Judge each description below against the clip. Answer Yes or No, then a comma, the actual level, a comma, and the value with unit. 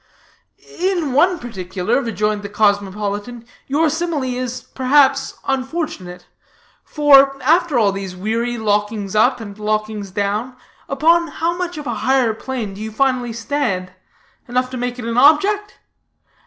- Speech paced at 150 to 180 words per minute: No, average, 140 wpm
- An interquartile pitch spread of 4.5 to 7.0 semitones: Yes, average, 5.1 semitones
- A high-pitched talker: Yes, high, 245 Hz